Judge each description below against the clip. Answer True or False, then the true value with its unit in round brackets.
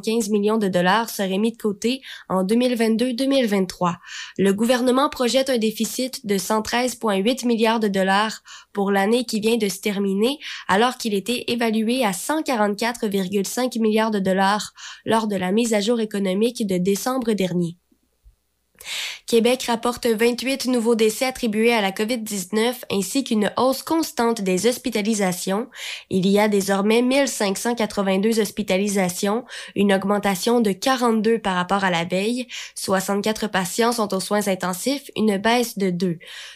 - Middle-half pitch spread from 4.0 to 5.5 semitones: False (3.4 semitones)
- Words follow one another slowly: True (140 wpm)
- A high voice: True (220 Hz)